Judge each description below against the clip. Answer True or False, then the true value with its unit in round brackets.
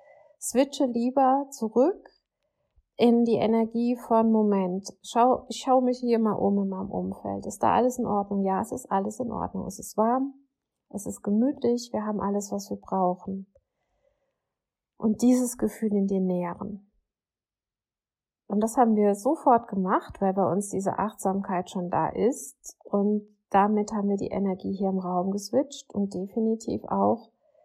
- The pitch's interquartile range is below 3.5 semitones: False (3.8 semitones)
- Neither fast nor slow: True (160 wpm)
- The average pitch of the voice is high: True (210 Hz)